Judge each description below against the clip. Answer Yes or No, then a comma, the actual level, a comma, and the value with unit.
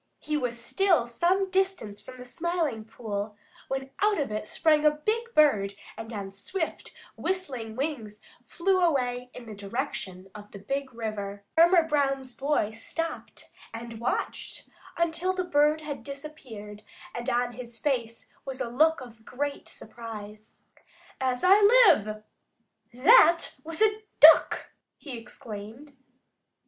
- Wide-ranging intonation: Yes, wide, 6.3 semitones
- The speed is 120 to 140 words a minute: Yes, slow, 135 wpm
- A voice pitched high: Yes, very high, 260 Hz